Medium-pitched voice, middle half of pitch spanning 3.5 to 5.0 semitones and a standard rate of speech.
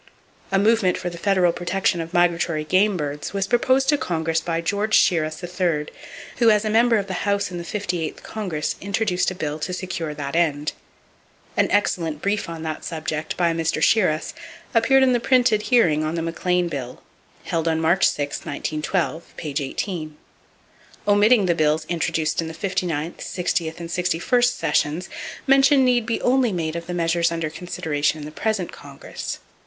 Yes: medium, 175 Hz; average, 4.2 semitones; average, 175 wpm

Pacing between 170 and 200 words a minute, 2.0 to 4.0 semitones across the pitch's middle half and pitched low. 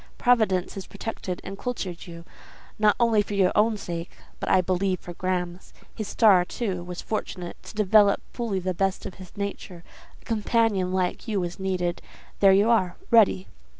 No: average, 175 wpm; average, 2.9 semitones; high, 190 Hz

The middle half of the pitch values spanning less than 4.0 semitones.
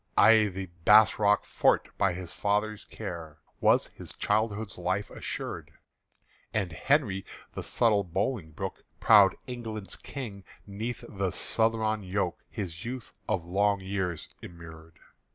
Yes: average, 3.1 semitones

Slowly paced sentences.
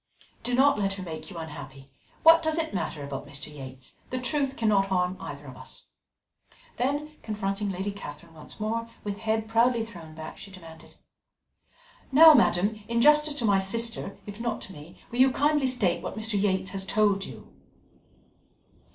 No: average, 175 wpm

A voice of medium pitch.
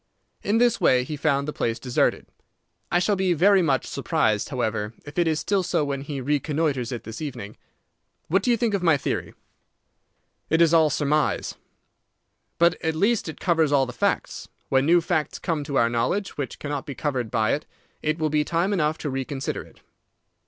Yes: medium, 150 Hz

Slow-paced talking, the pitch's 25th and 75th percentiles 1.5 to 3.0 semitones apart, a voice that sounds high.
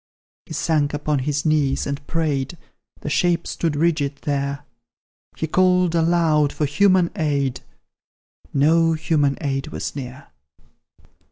No: slow, 120 wpm; average, 2.7 semitones; medium, 150 Hz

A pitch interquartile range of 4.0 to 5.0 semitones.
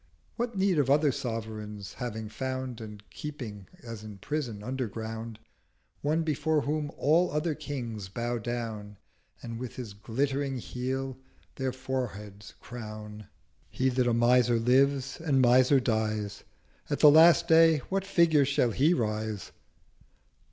Yes: average, 4.7 semitones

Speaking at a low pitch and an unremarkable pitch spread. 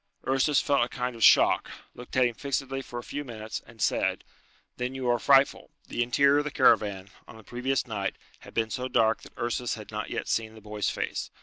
Yes: low, 120 Hz; average, 3.1 semitones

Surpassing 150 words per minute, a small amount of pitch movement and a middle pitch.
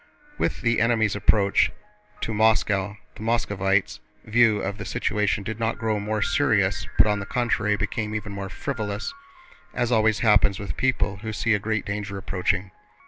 No: average, 165 wpm; narrow, 1.8 semitones; low, 105 Hz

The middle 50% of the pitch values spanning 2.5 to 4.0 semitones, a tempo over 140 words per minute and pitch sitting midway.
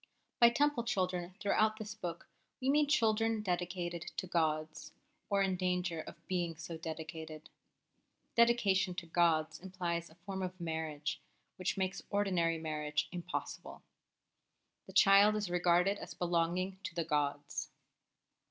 No: average, 3.2 semitones; slow, 135 wpm; medium, 180 Hz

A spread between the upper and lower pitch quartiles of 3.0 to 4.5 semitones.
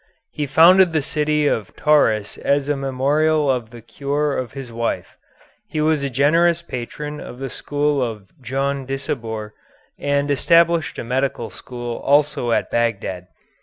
Yes: average, 3.8 semitones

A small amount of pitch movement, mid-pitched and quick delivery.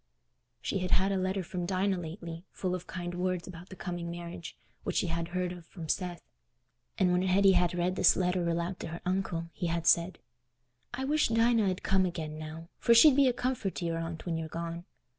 Yes: narrow, 2.0 semitones; medium, 180 Hz; fast, 215 wpm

